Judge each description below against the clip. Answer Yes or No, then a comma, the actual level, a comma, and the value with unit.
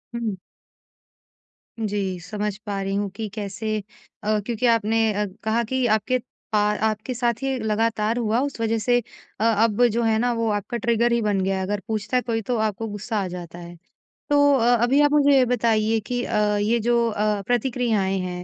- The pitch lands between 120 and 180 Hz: No, high, 220 Hz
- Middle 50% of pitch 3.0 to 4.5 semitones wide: No, narrow, 2.4 semitones